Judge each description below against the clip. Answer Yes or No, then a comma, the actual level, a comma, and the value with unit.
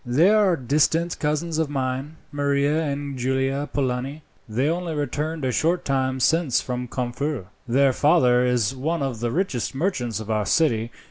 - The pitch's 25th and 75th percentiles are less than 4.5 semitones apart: Yes, average, 3.8 semitones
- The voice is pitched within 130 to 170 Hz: Yes, medium, 140 Hz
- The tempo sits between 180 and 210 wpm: No, average, 160 wpm